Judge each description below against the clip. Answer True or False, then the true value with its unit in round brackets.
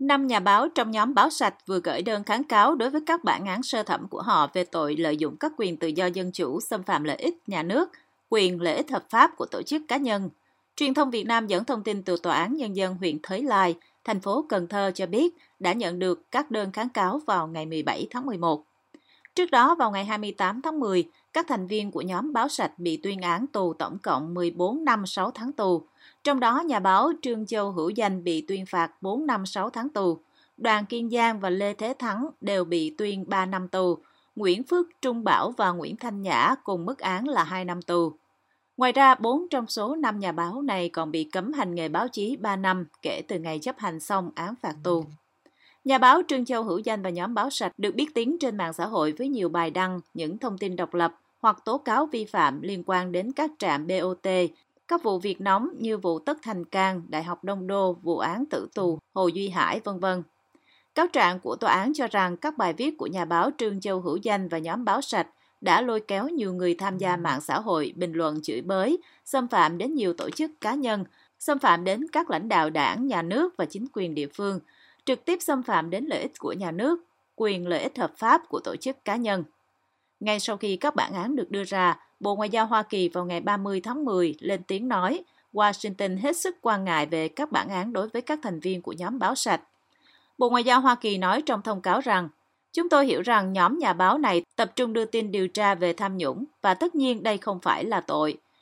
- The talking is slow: False (235 wpm)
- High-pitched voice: True (200 Hz)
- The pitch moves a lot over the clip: True (6.0 semitones)